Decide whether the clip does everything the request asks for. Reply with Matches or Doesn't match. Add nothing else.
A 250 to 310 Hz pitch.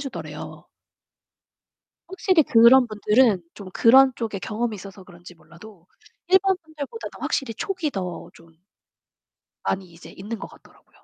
Doesn't match